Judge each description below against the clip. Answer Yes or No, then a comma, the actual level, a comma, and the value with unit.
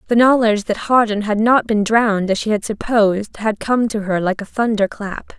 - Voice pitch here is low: No, high, 215 Hz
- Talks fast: Yes, fast, 210 wpm